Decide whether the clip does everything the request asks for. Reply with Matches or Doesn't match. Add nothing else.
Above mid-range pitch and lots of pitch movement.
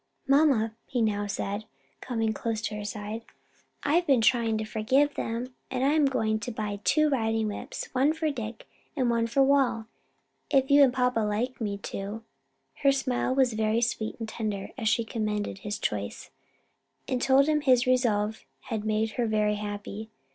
Doesn't match